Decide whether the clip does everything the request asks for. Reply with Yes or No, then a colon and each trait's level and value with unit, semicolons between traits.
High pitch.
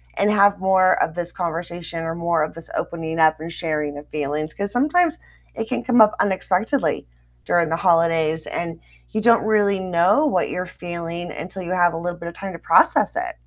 No: medium, 175 Hz